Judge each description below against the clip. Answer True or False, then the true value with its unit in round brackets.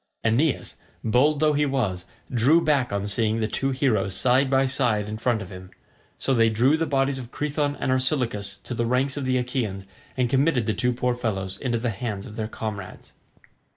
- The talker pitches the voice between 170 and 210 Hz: False (125 Hz)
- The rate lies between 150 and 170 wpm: False (200 wpm)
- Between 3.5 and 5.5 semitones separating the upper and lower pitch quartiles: True (3.9 semitones)